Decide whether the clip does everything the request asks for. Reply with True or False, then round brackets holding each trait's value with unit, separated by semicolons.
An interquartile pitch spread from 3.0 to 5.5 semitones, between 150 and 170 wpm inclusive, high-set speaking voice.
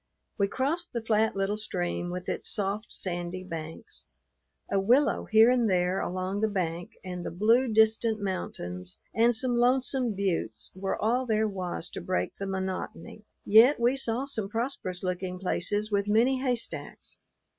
True (4.1 semitones; 155 wpm; 205 Hz)